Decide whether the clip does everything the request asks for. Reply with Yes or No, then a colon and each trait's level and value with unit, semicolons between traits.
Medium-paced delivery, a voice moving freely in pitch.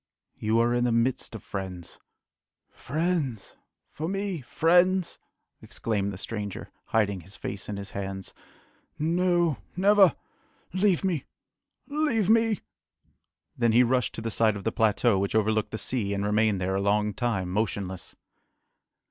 Yes: average, 145 wpm; wide, 8.8 semitones